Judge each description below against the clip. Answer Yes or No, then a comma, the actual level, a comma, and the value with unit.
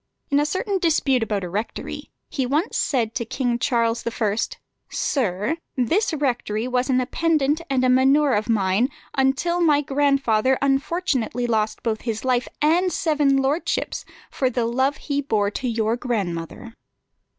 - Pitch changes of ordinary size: Yes, average, 4.0 semitones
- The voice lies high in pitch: Yes, very high, 255 Hz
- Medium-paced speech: Yes, average, 150 wpm